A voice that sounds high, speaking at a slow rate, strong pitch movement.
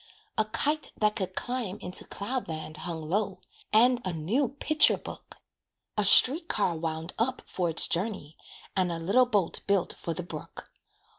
No: high, 195 Hz; average, 165 wpm; wide, 6.3 semitones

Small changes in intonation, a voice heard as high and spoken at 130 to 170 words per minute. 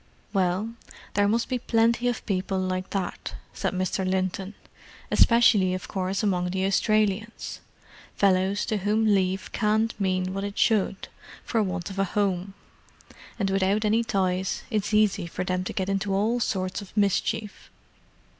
Yes: narrow, 2.3 semitones; high, 195 Hz; average, 155 wpm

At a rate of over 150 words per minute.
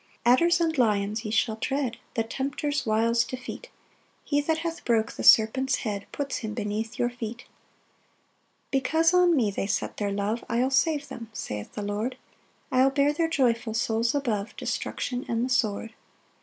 Yes: average, 170 wpm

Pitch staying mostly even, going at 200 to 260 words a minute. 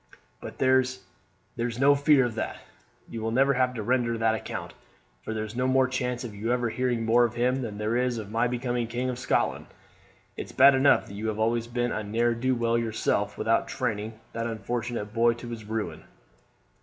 Yes: narrow, 2.1 semitones; fast, 205 wpm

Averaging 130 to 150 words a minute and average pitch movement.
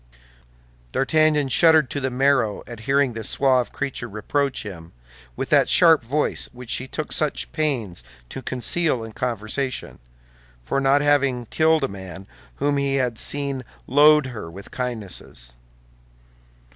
Yes: average, 140 wpm; average, 4.3 semitones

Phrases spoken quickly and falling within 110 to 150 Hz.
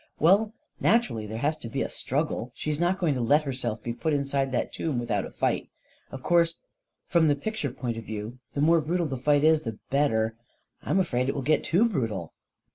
Yes: fast, 220 wpm; medium, 140 Hz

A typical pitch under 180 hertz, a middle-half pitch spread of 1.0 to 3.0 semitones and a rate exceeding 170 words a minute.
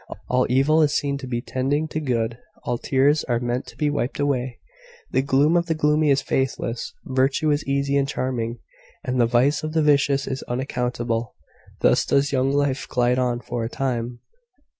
Yes: low, 135 Hz; average, 2.7 semitones; average, 185 wpm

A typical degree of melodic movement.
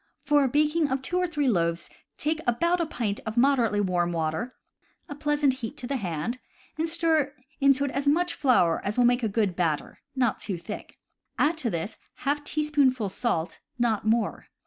No: wide, 6.2 semitones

